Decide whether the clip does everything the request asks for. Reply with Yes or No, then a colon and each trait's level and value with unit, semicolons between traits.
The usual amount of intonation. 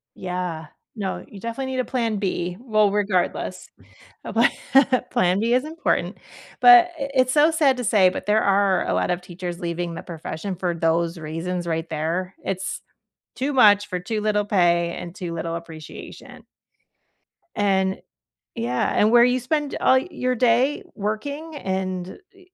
No: wide, 6.0 semitones